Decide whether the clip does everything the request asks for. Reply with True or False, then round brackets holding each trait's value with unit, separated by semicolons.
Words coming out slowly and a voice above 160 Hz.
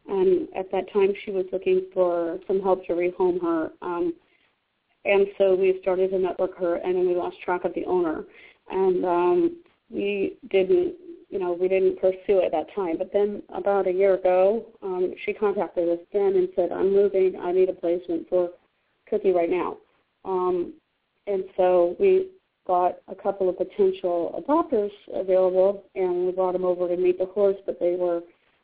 False (185 wpm; 190 Hz)